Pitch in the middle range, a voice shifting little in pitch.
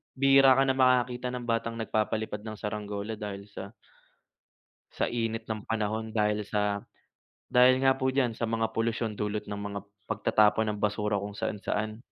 No: low, 110 Hz; narrow, 2.1 semitones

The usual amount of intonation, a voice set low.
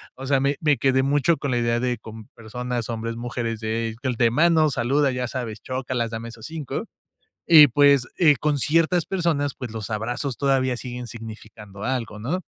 Yes: average, 3.7 semitones; low, 125 Hz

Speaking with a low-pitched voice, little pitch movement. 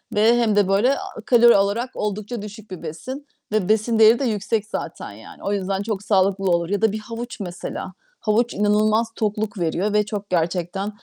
No: high, 210 Hz; narrow, 2.3 semitones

